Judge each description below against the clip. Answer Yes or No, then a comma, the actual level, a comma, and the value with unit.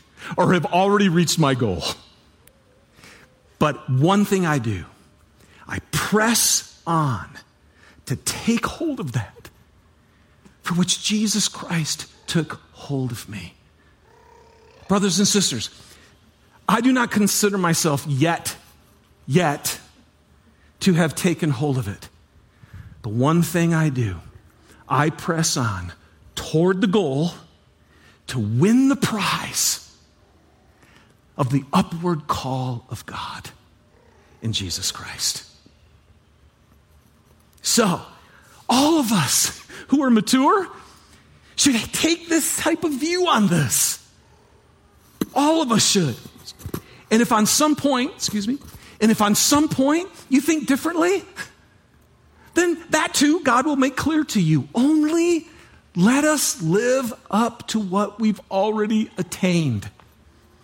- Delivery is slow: Yes, slow, 120 wpm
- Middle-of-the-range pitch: Yes, medium, 175 Hz